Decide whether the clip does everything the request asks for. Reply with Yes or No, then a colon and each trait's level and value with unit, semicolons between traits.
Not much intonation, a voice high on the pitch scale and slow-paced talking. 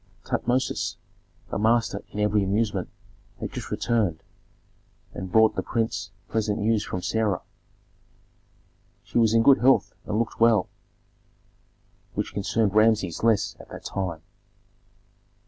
No: narrow, 2.3 semitones; low, 110 Hz; slow, 125 wpm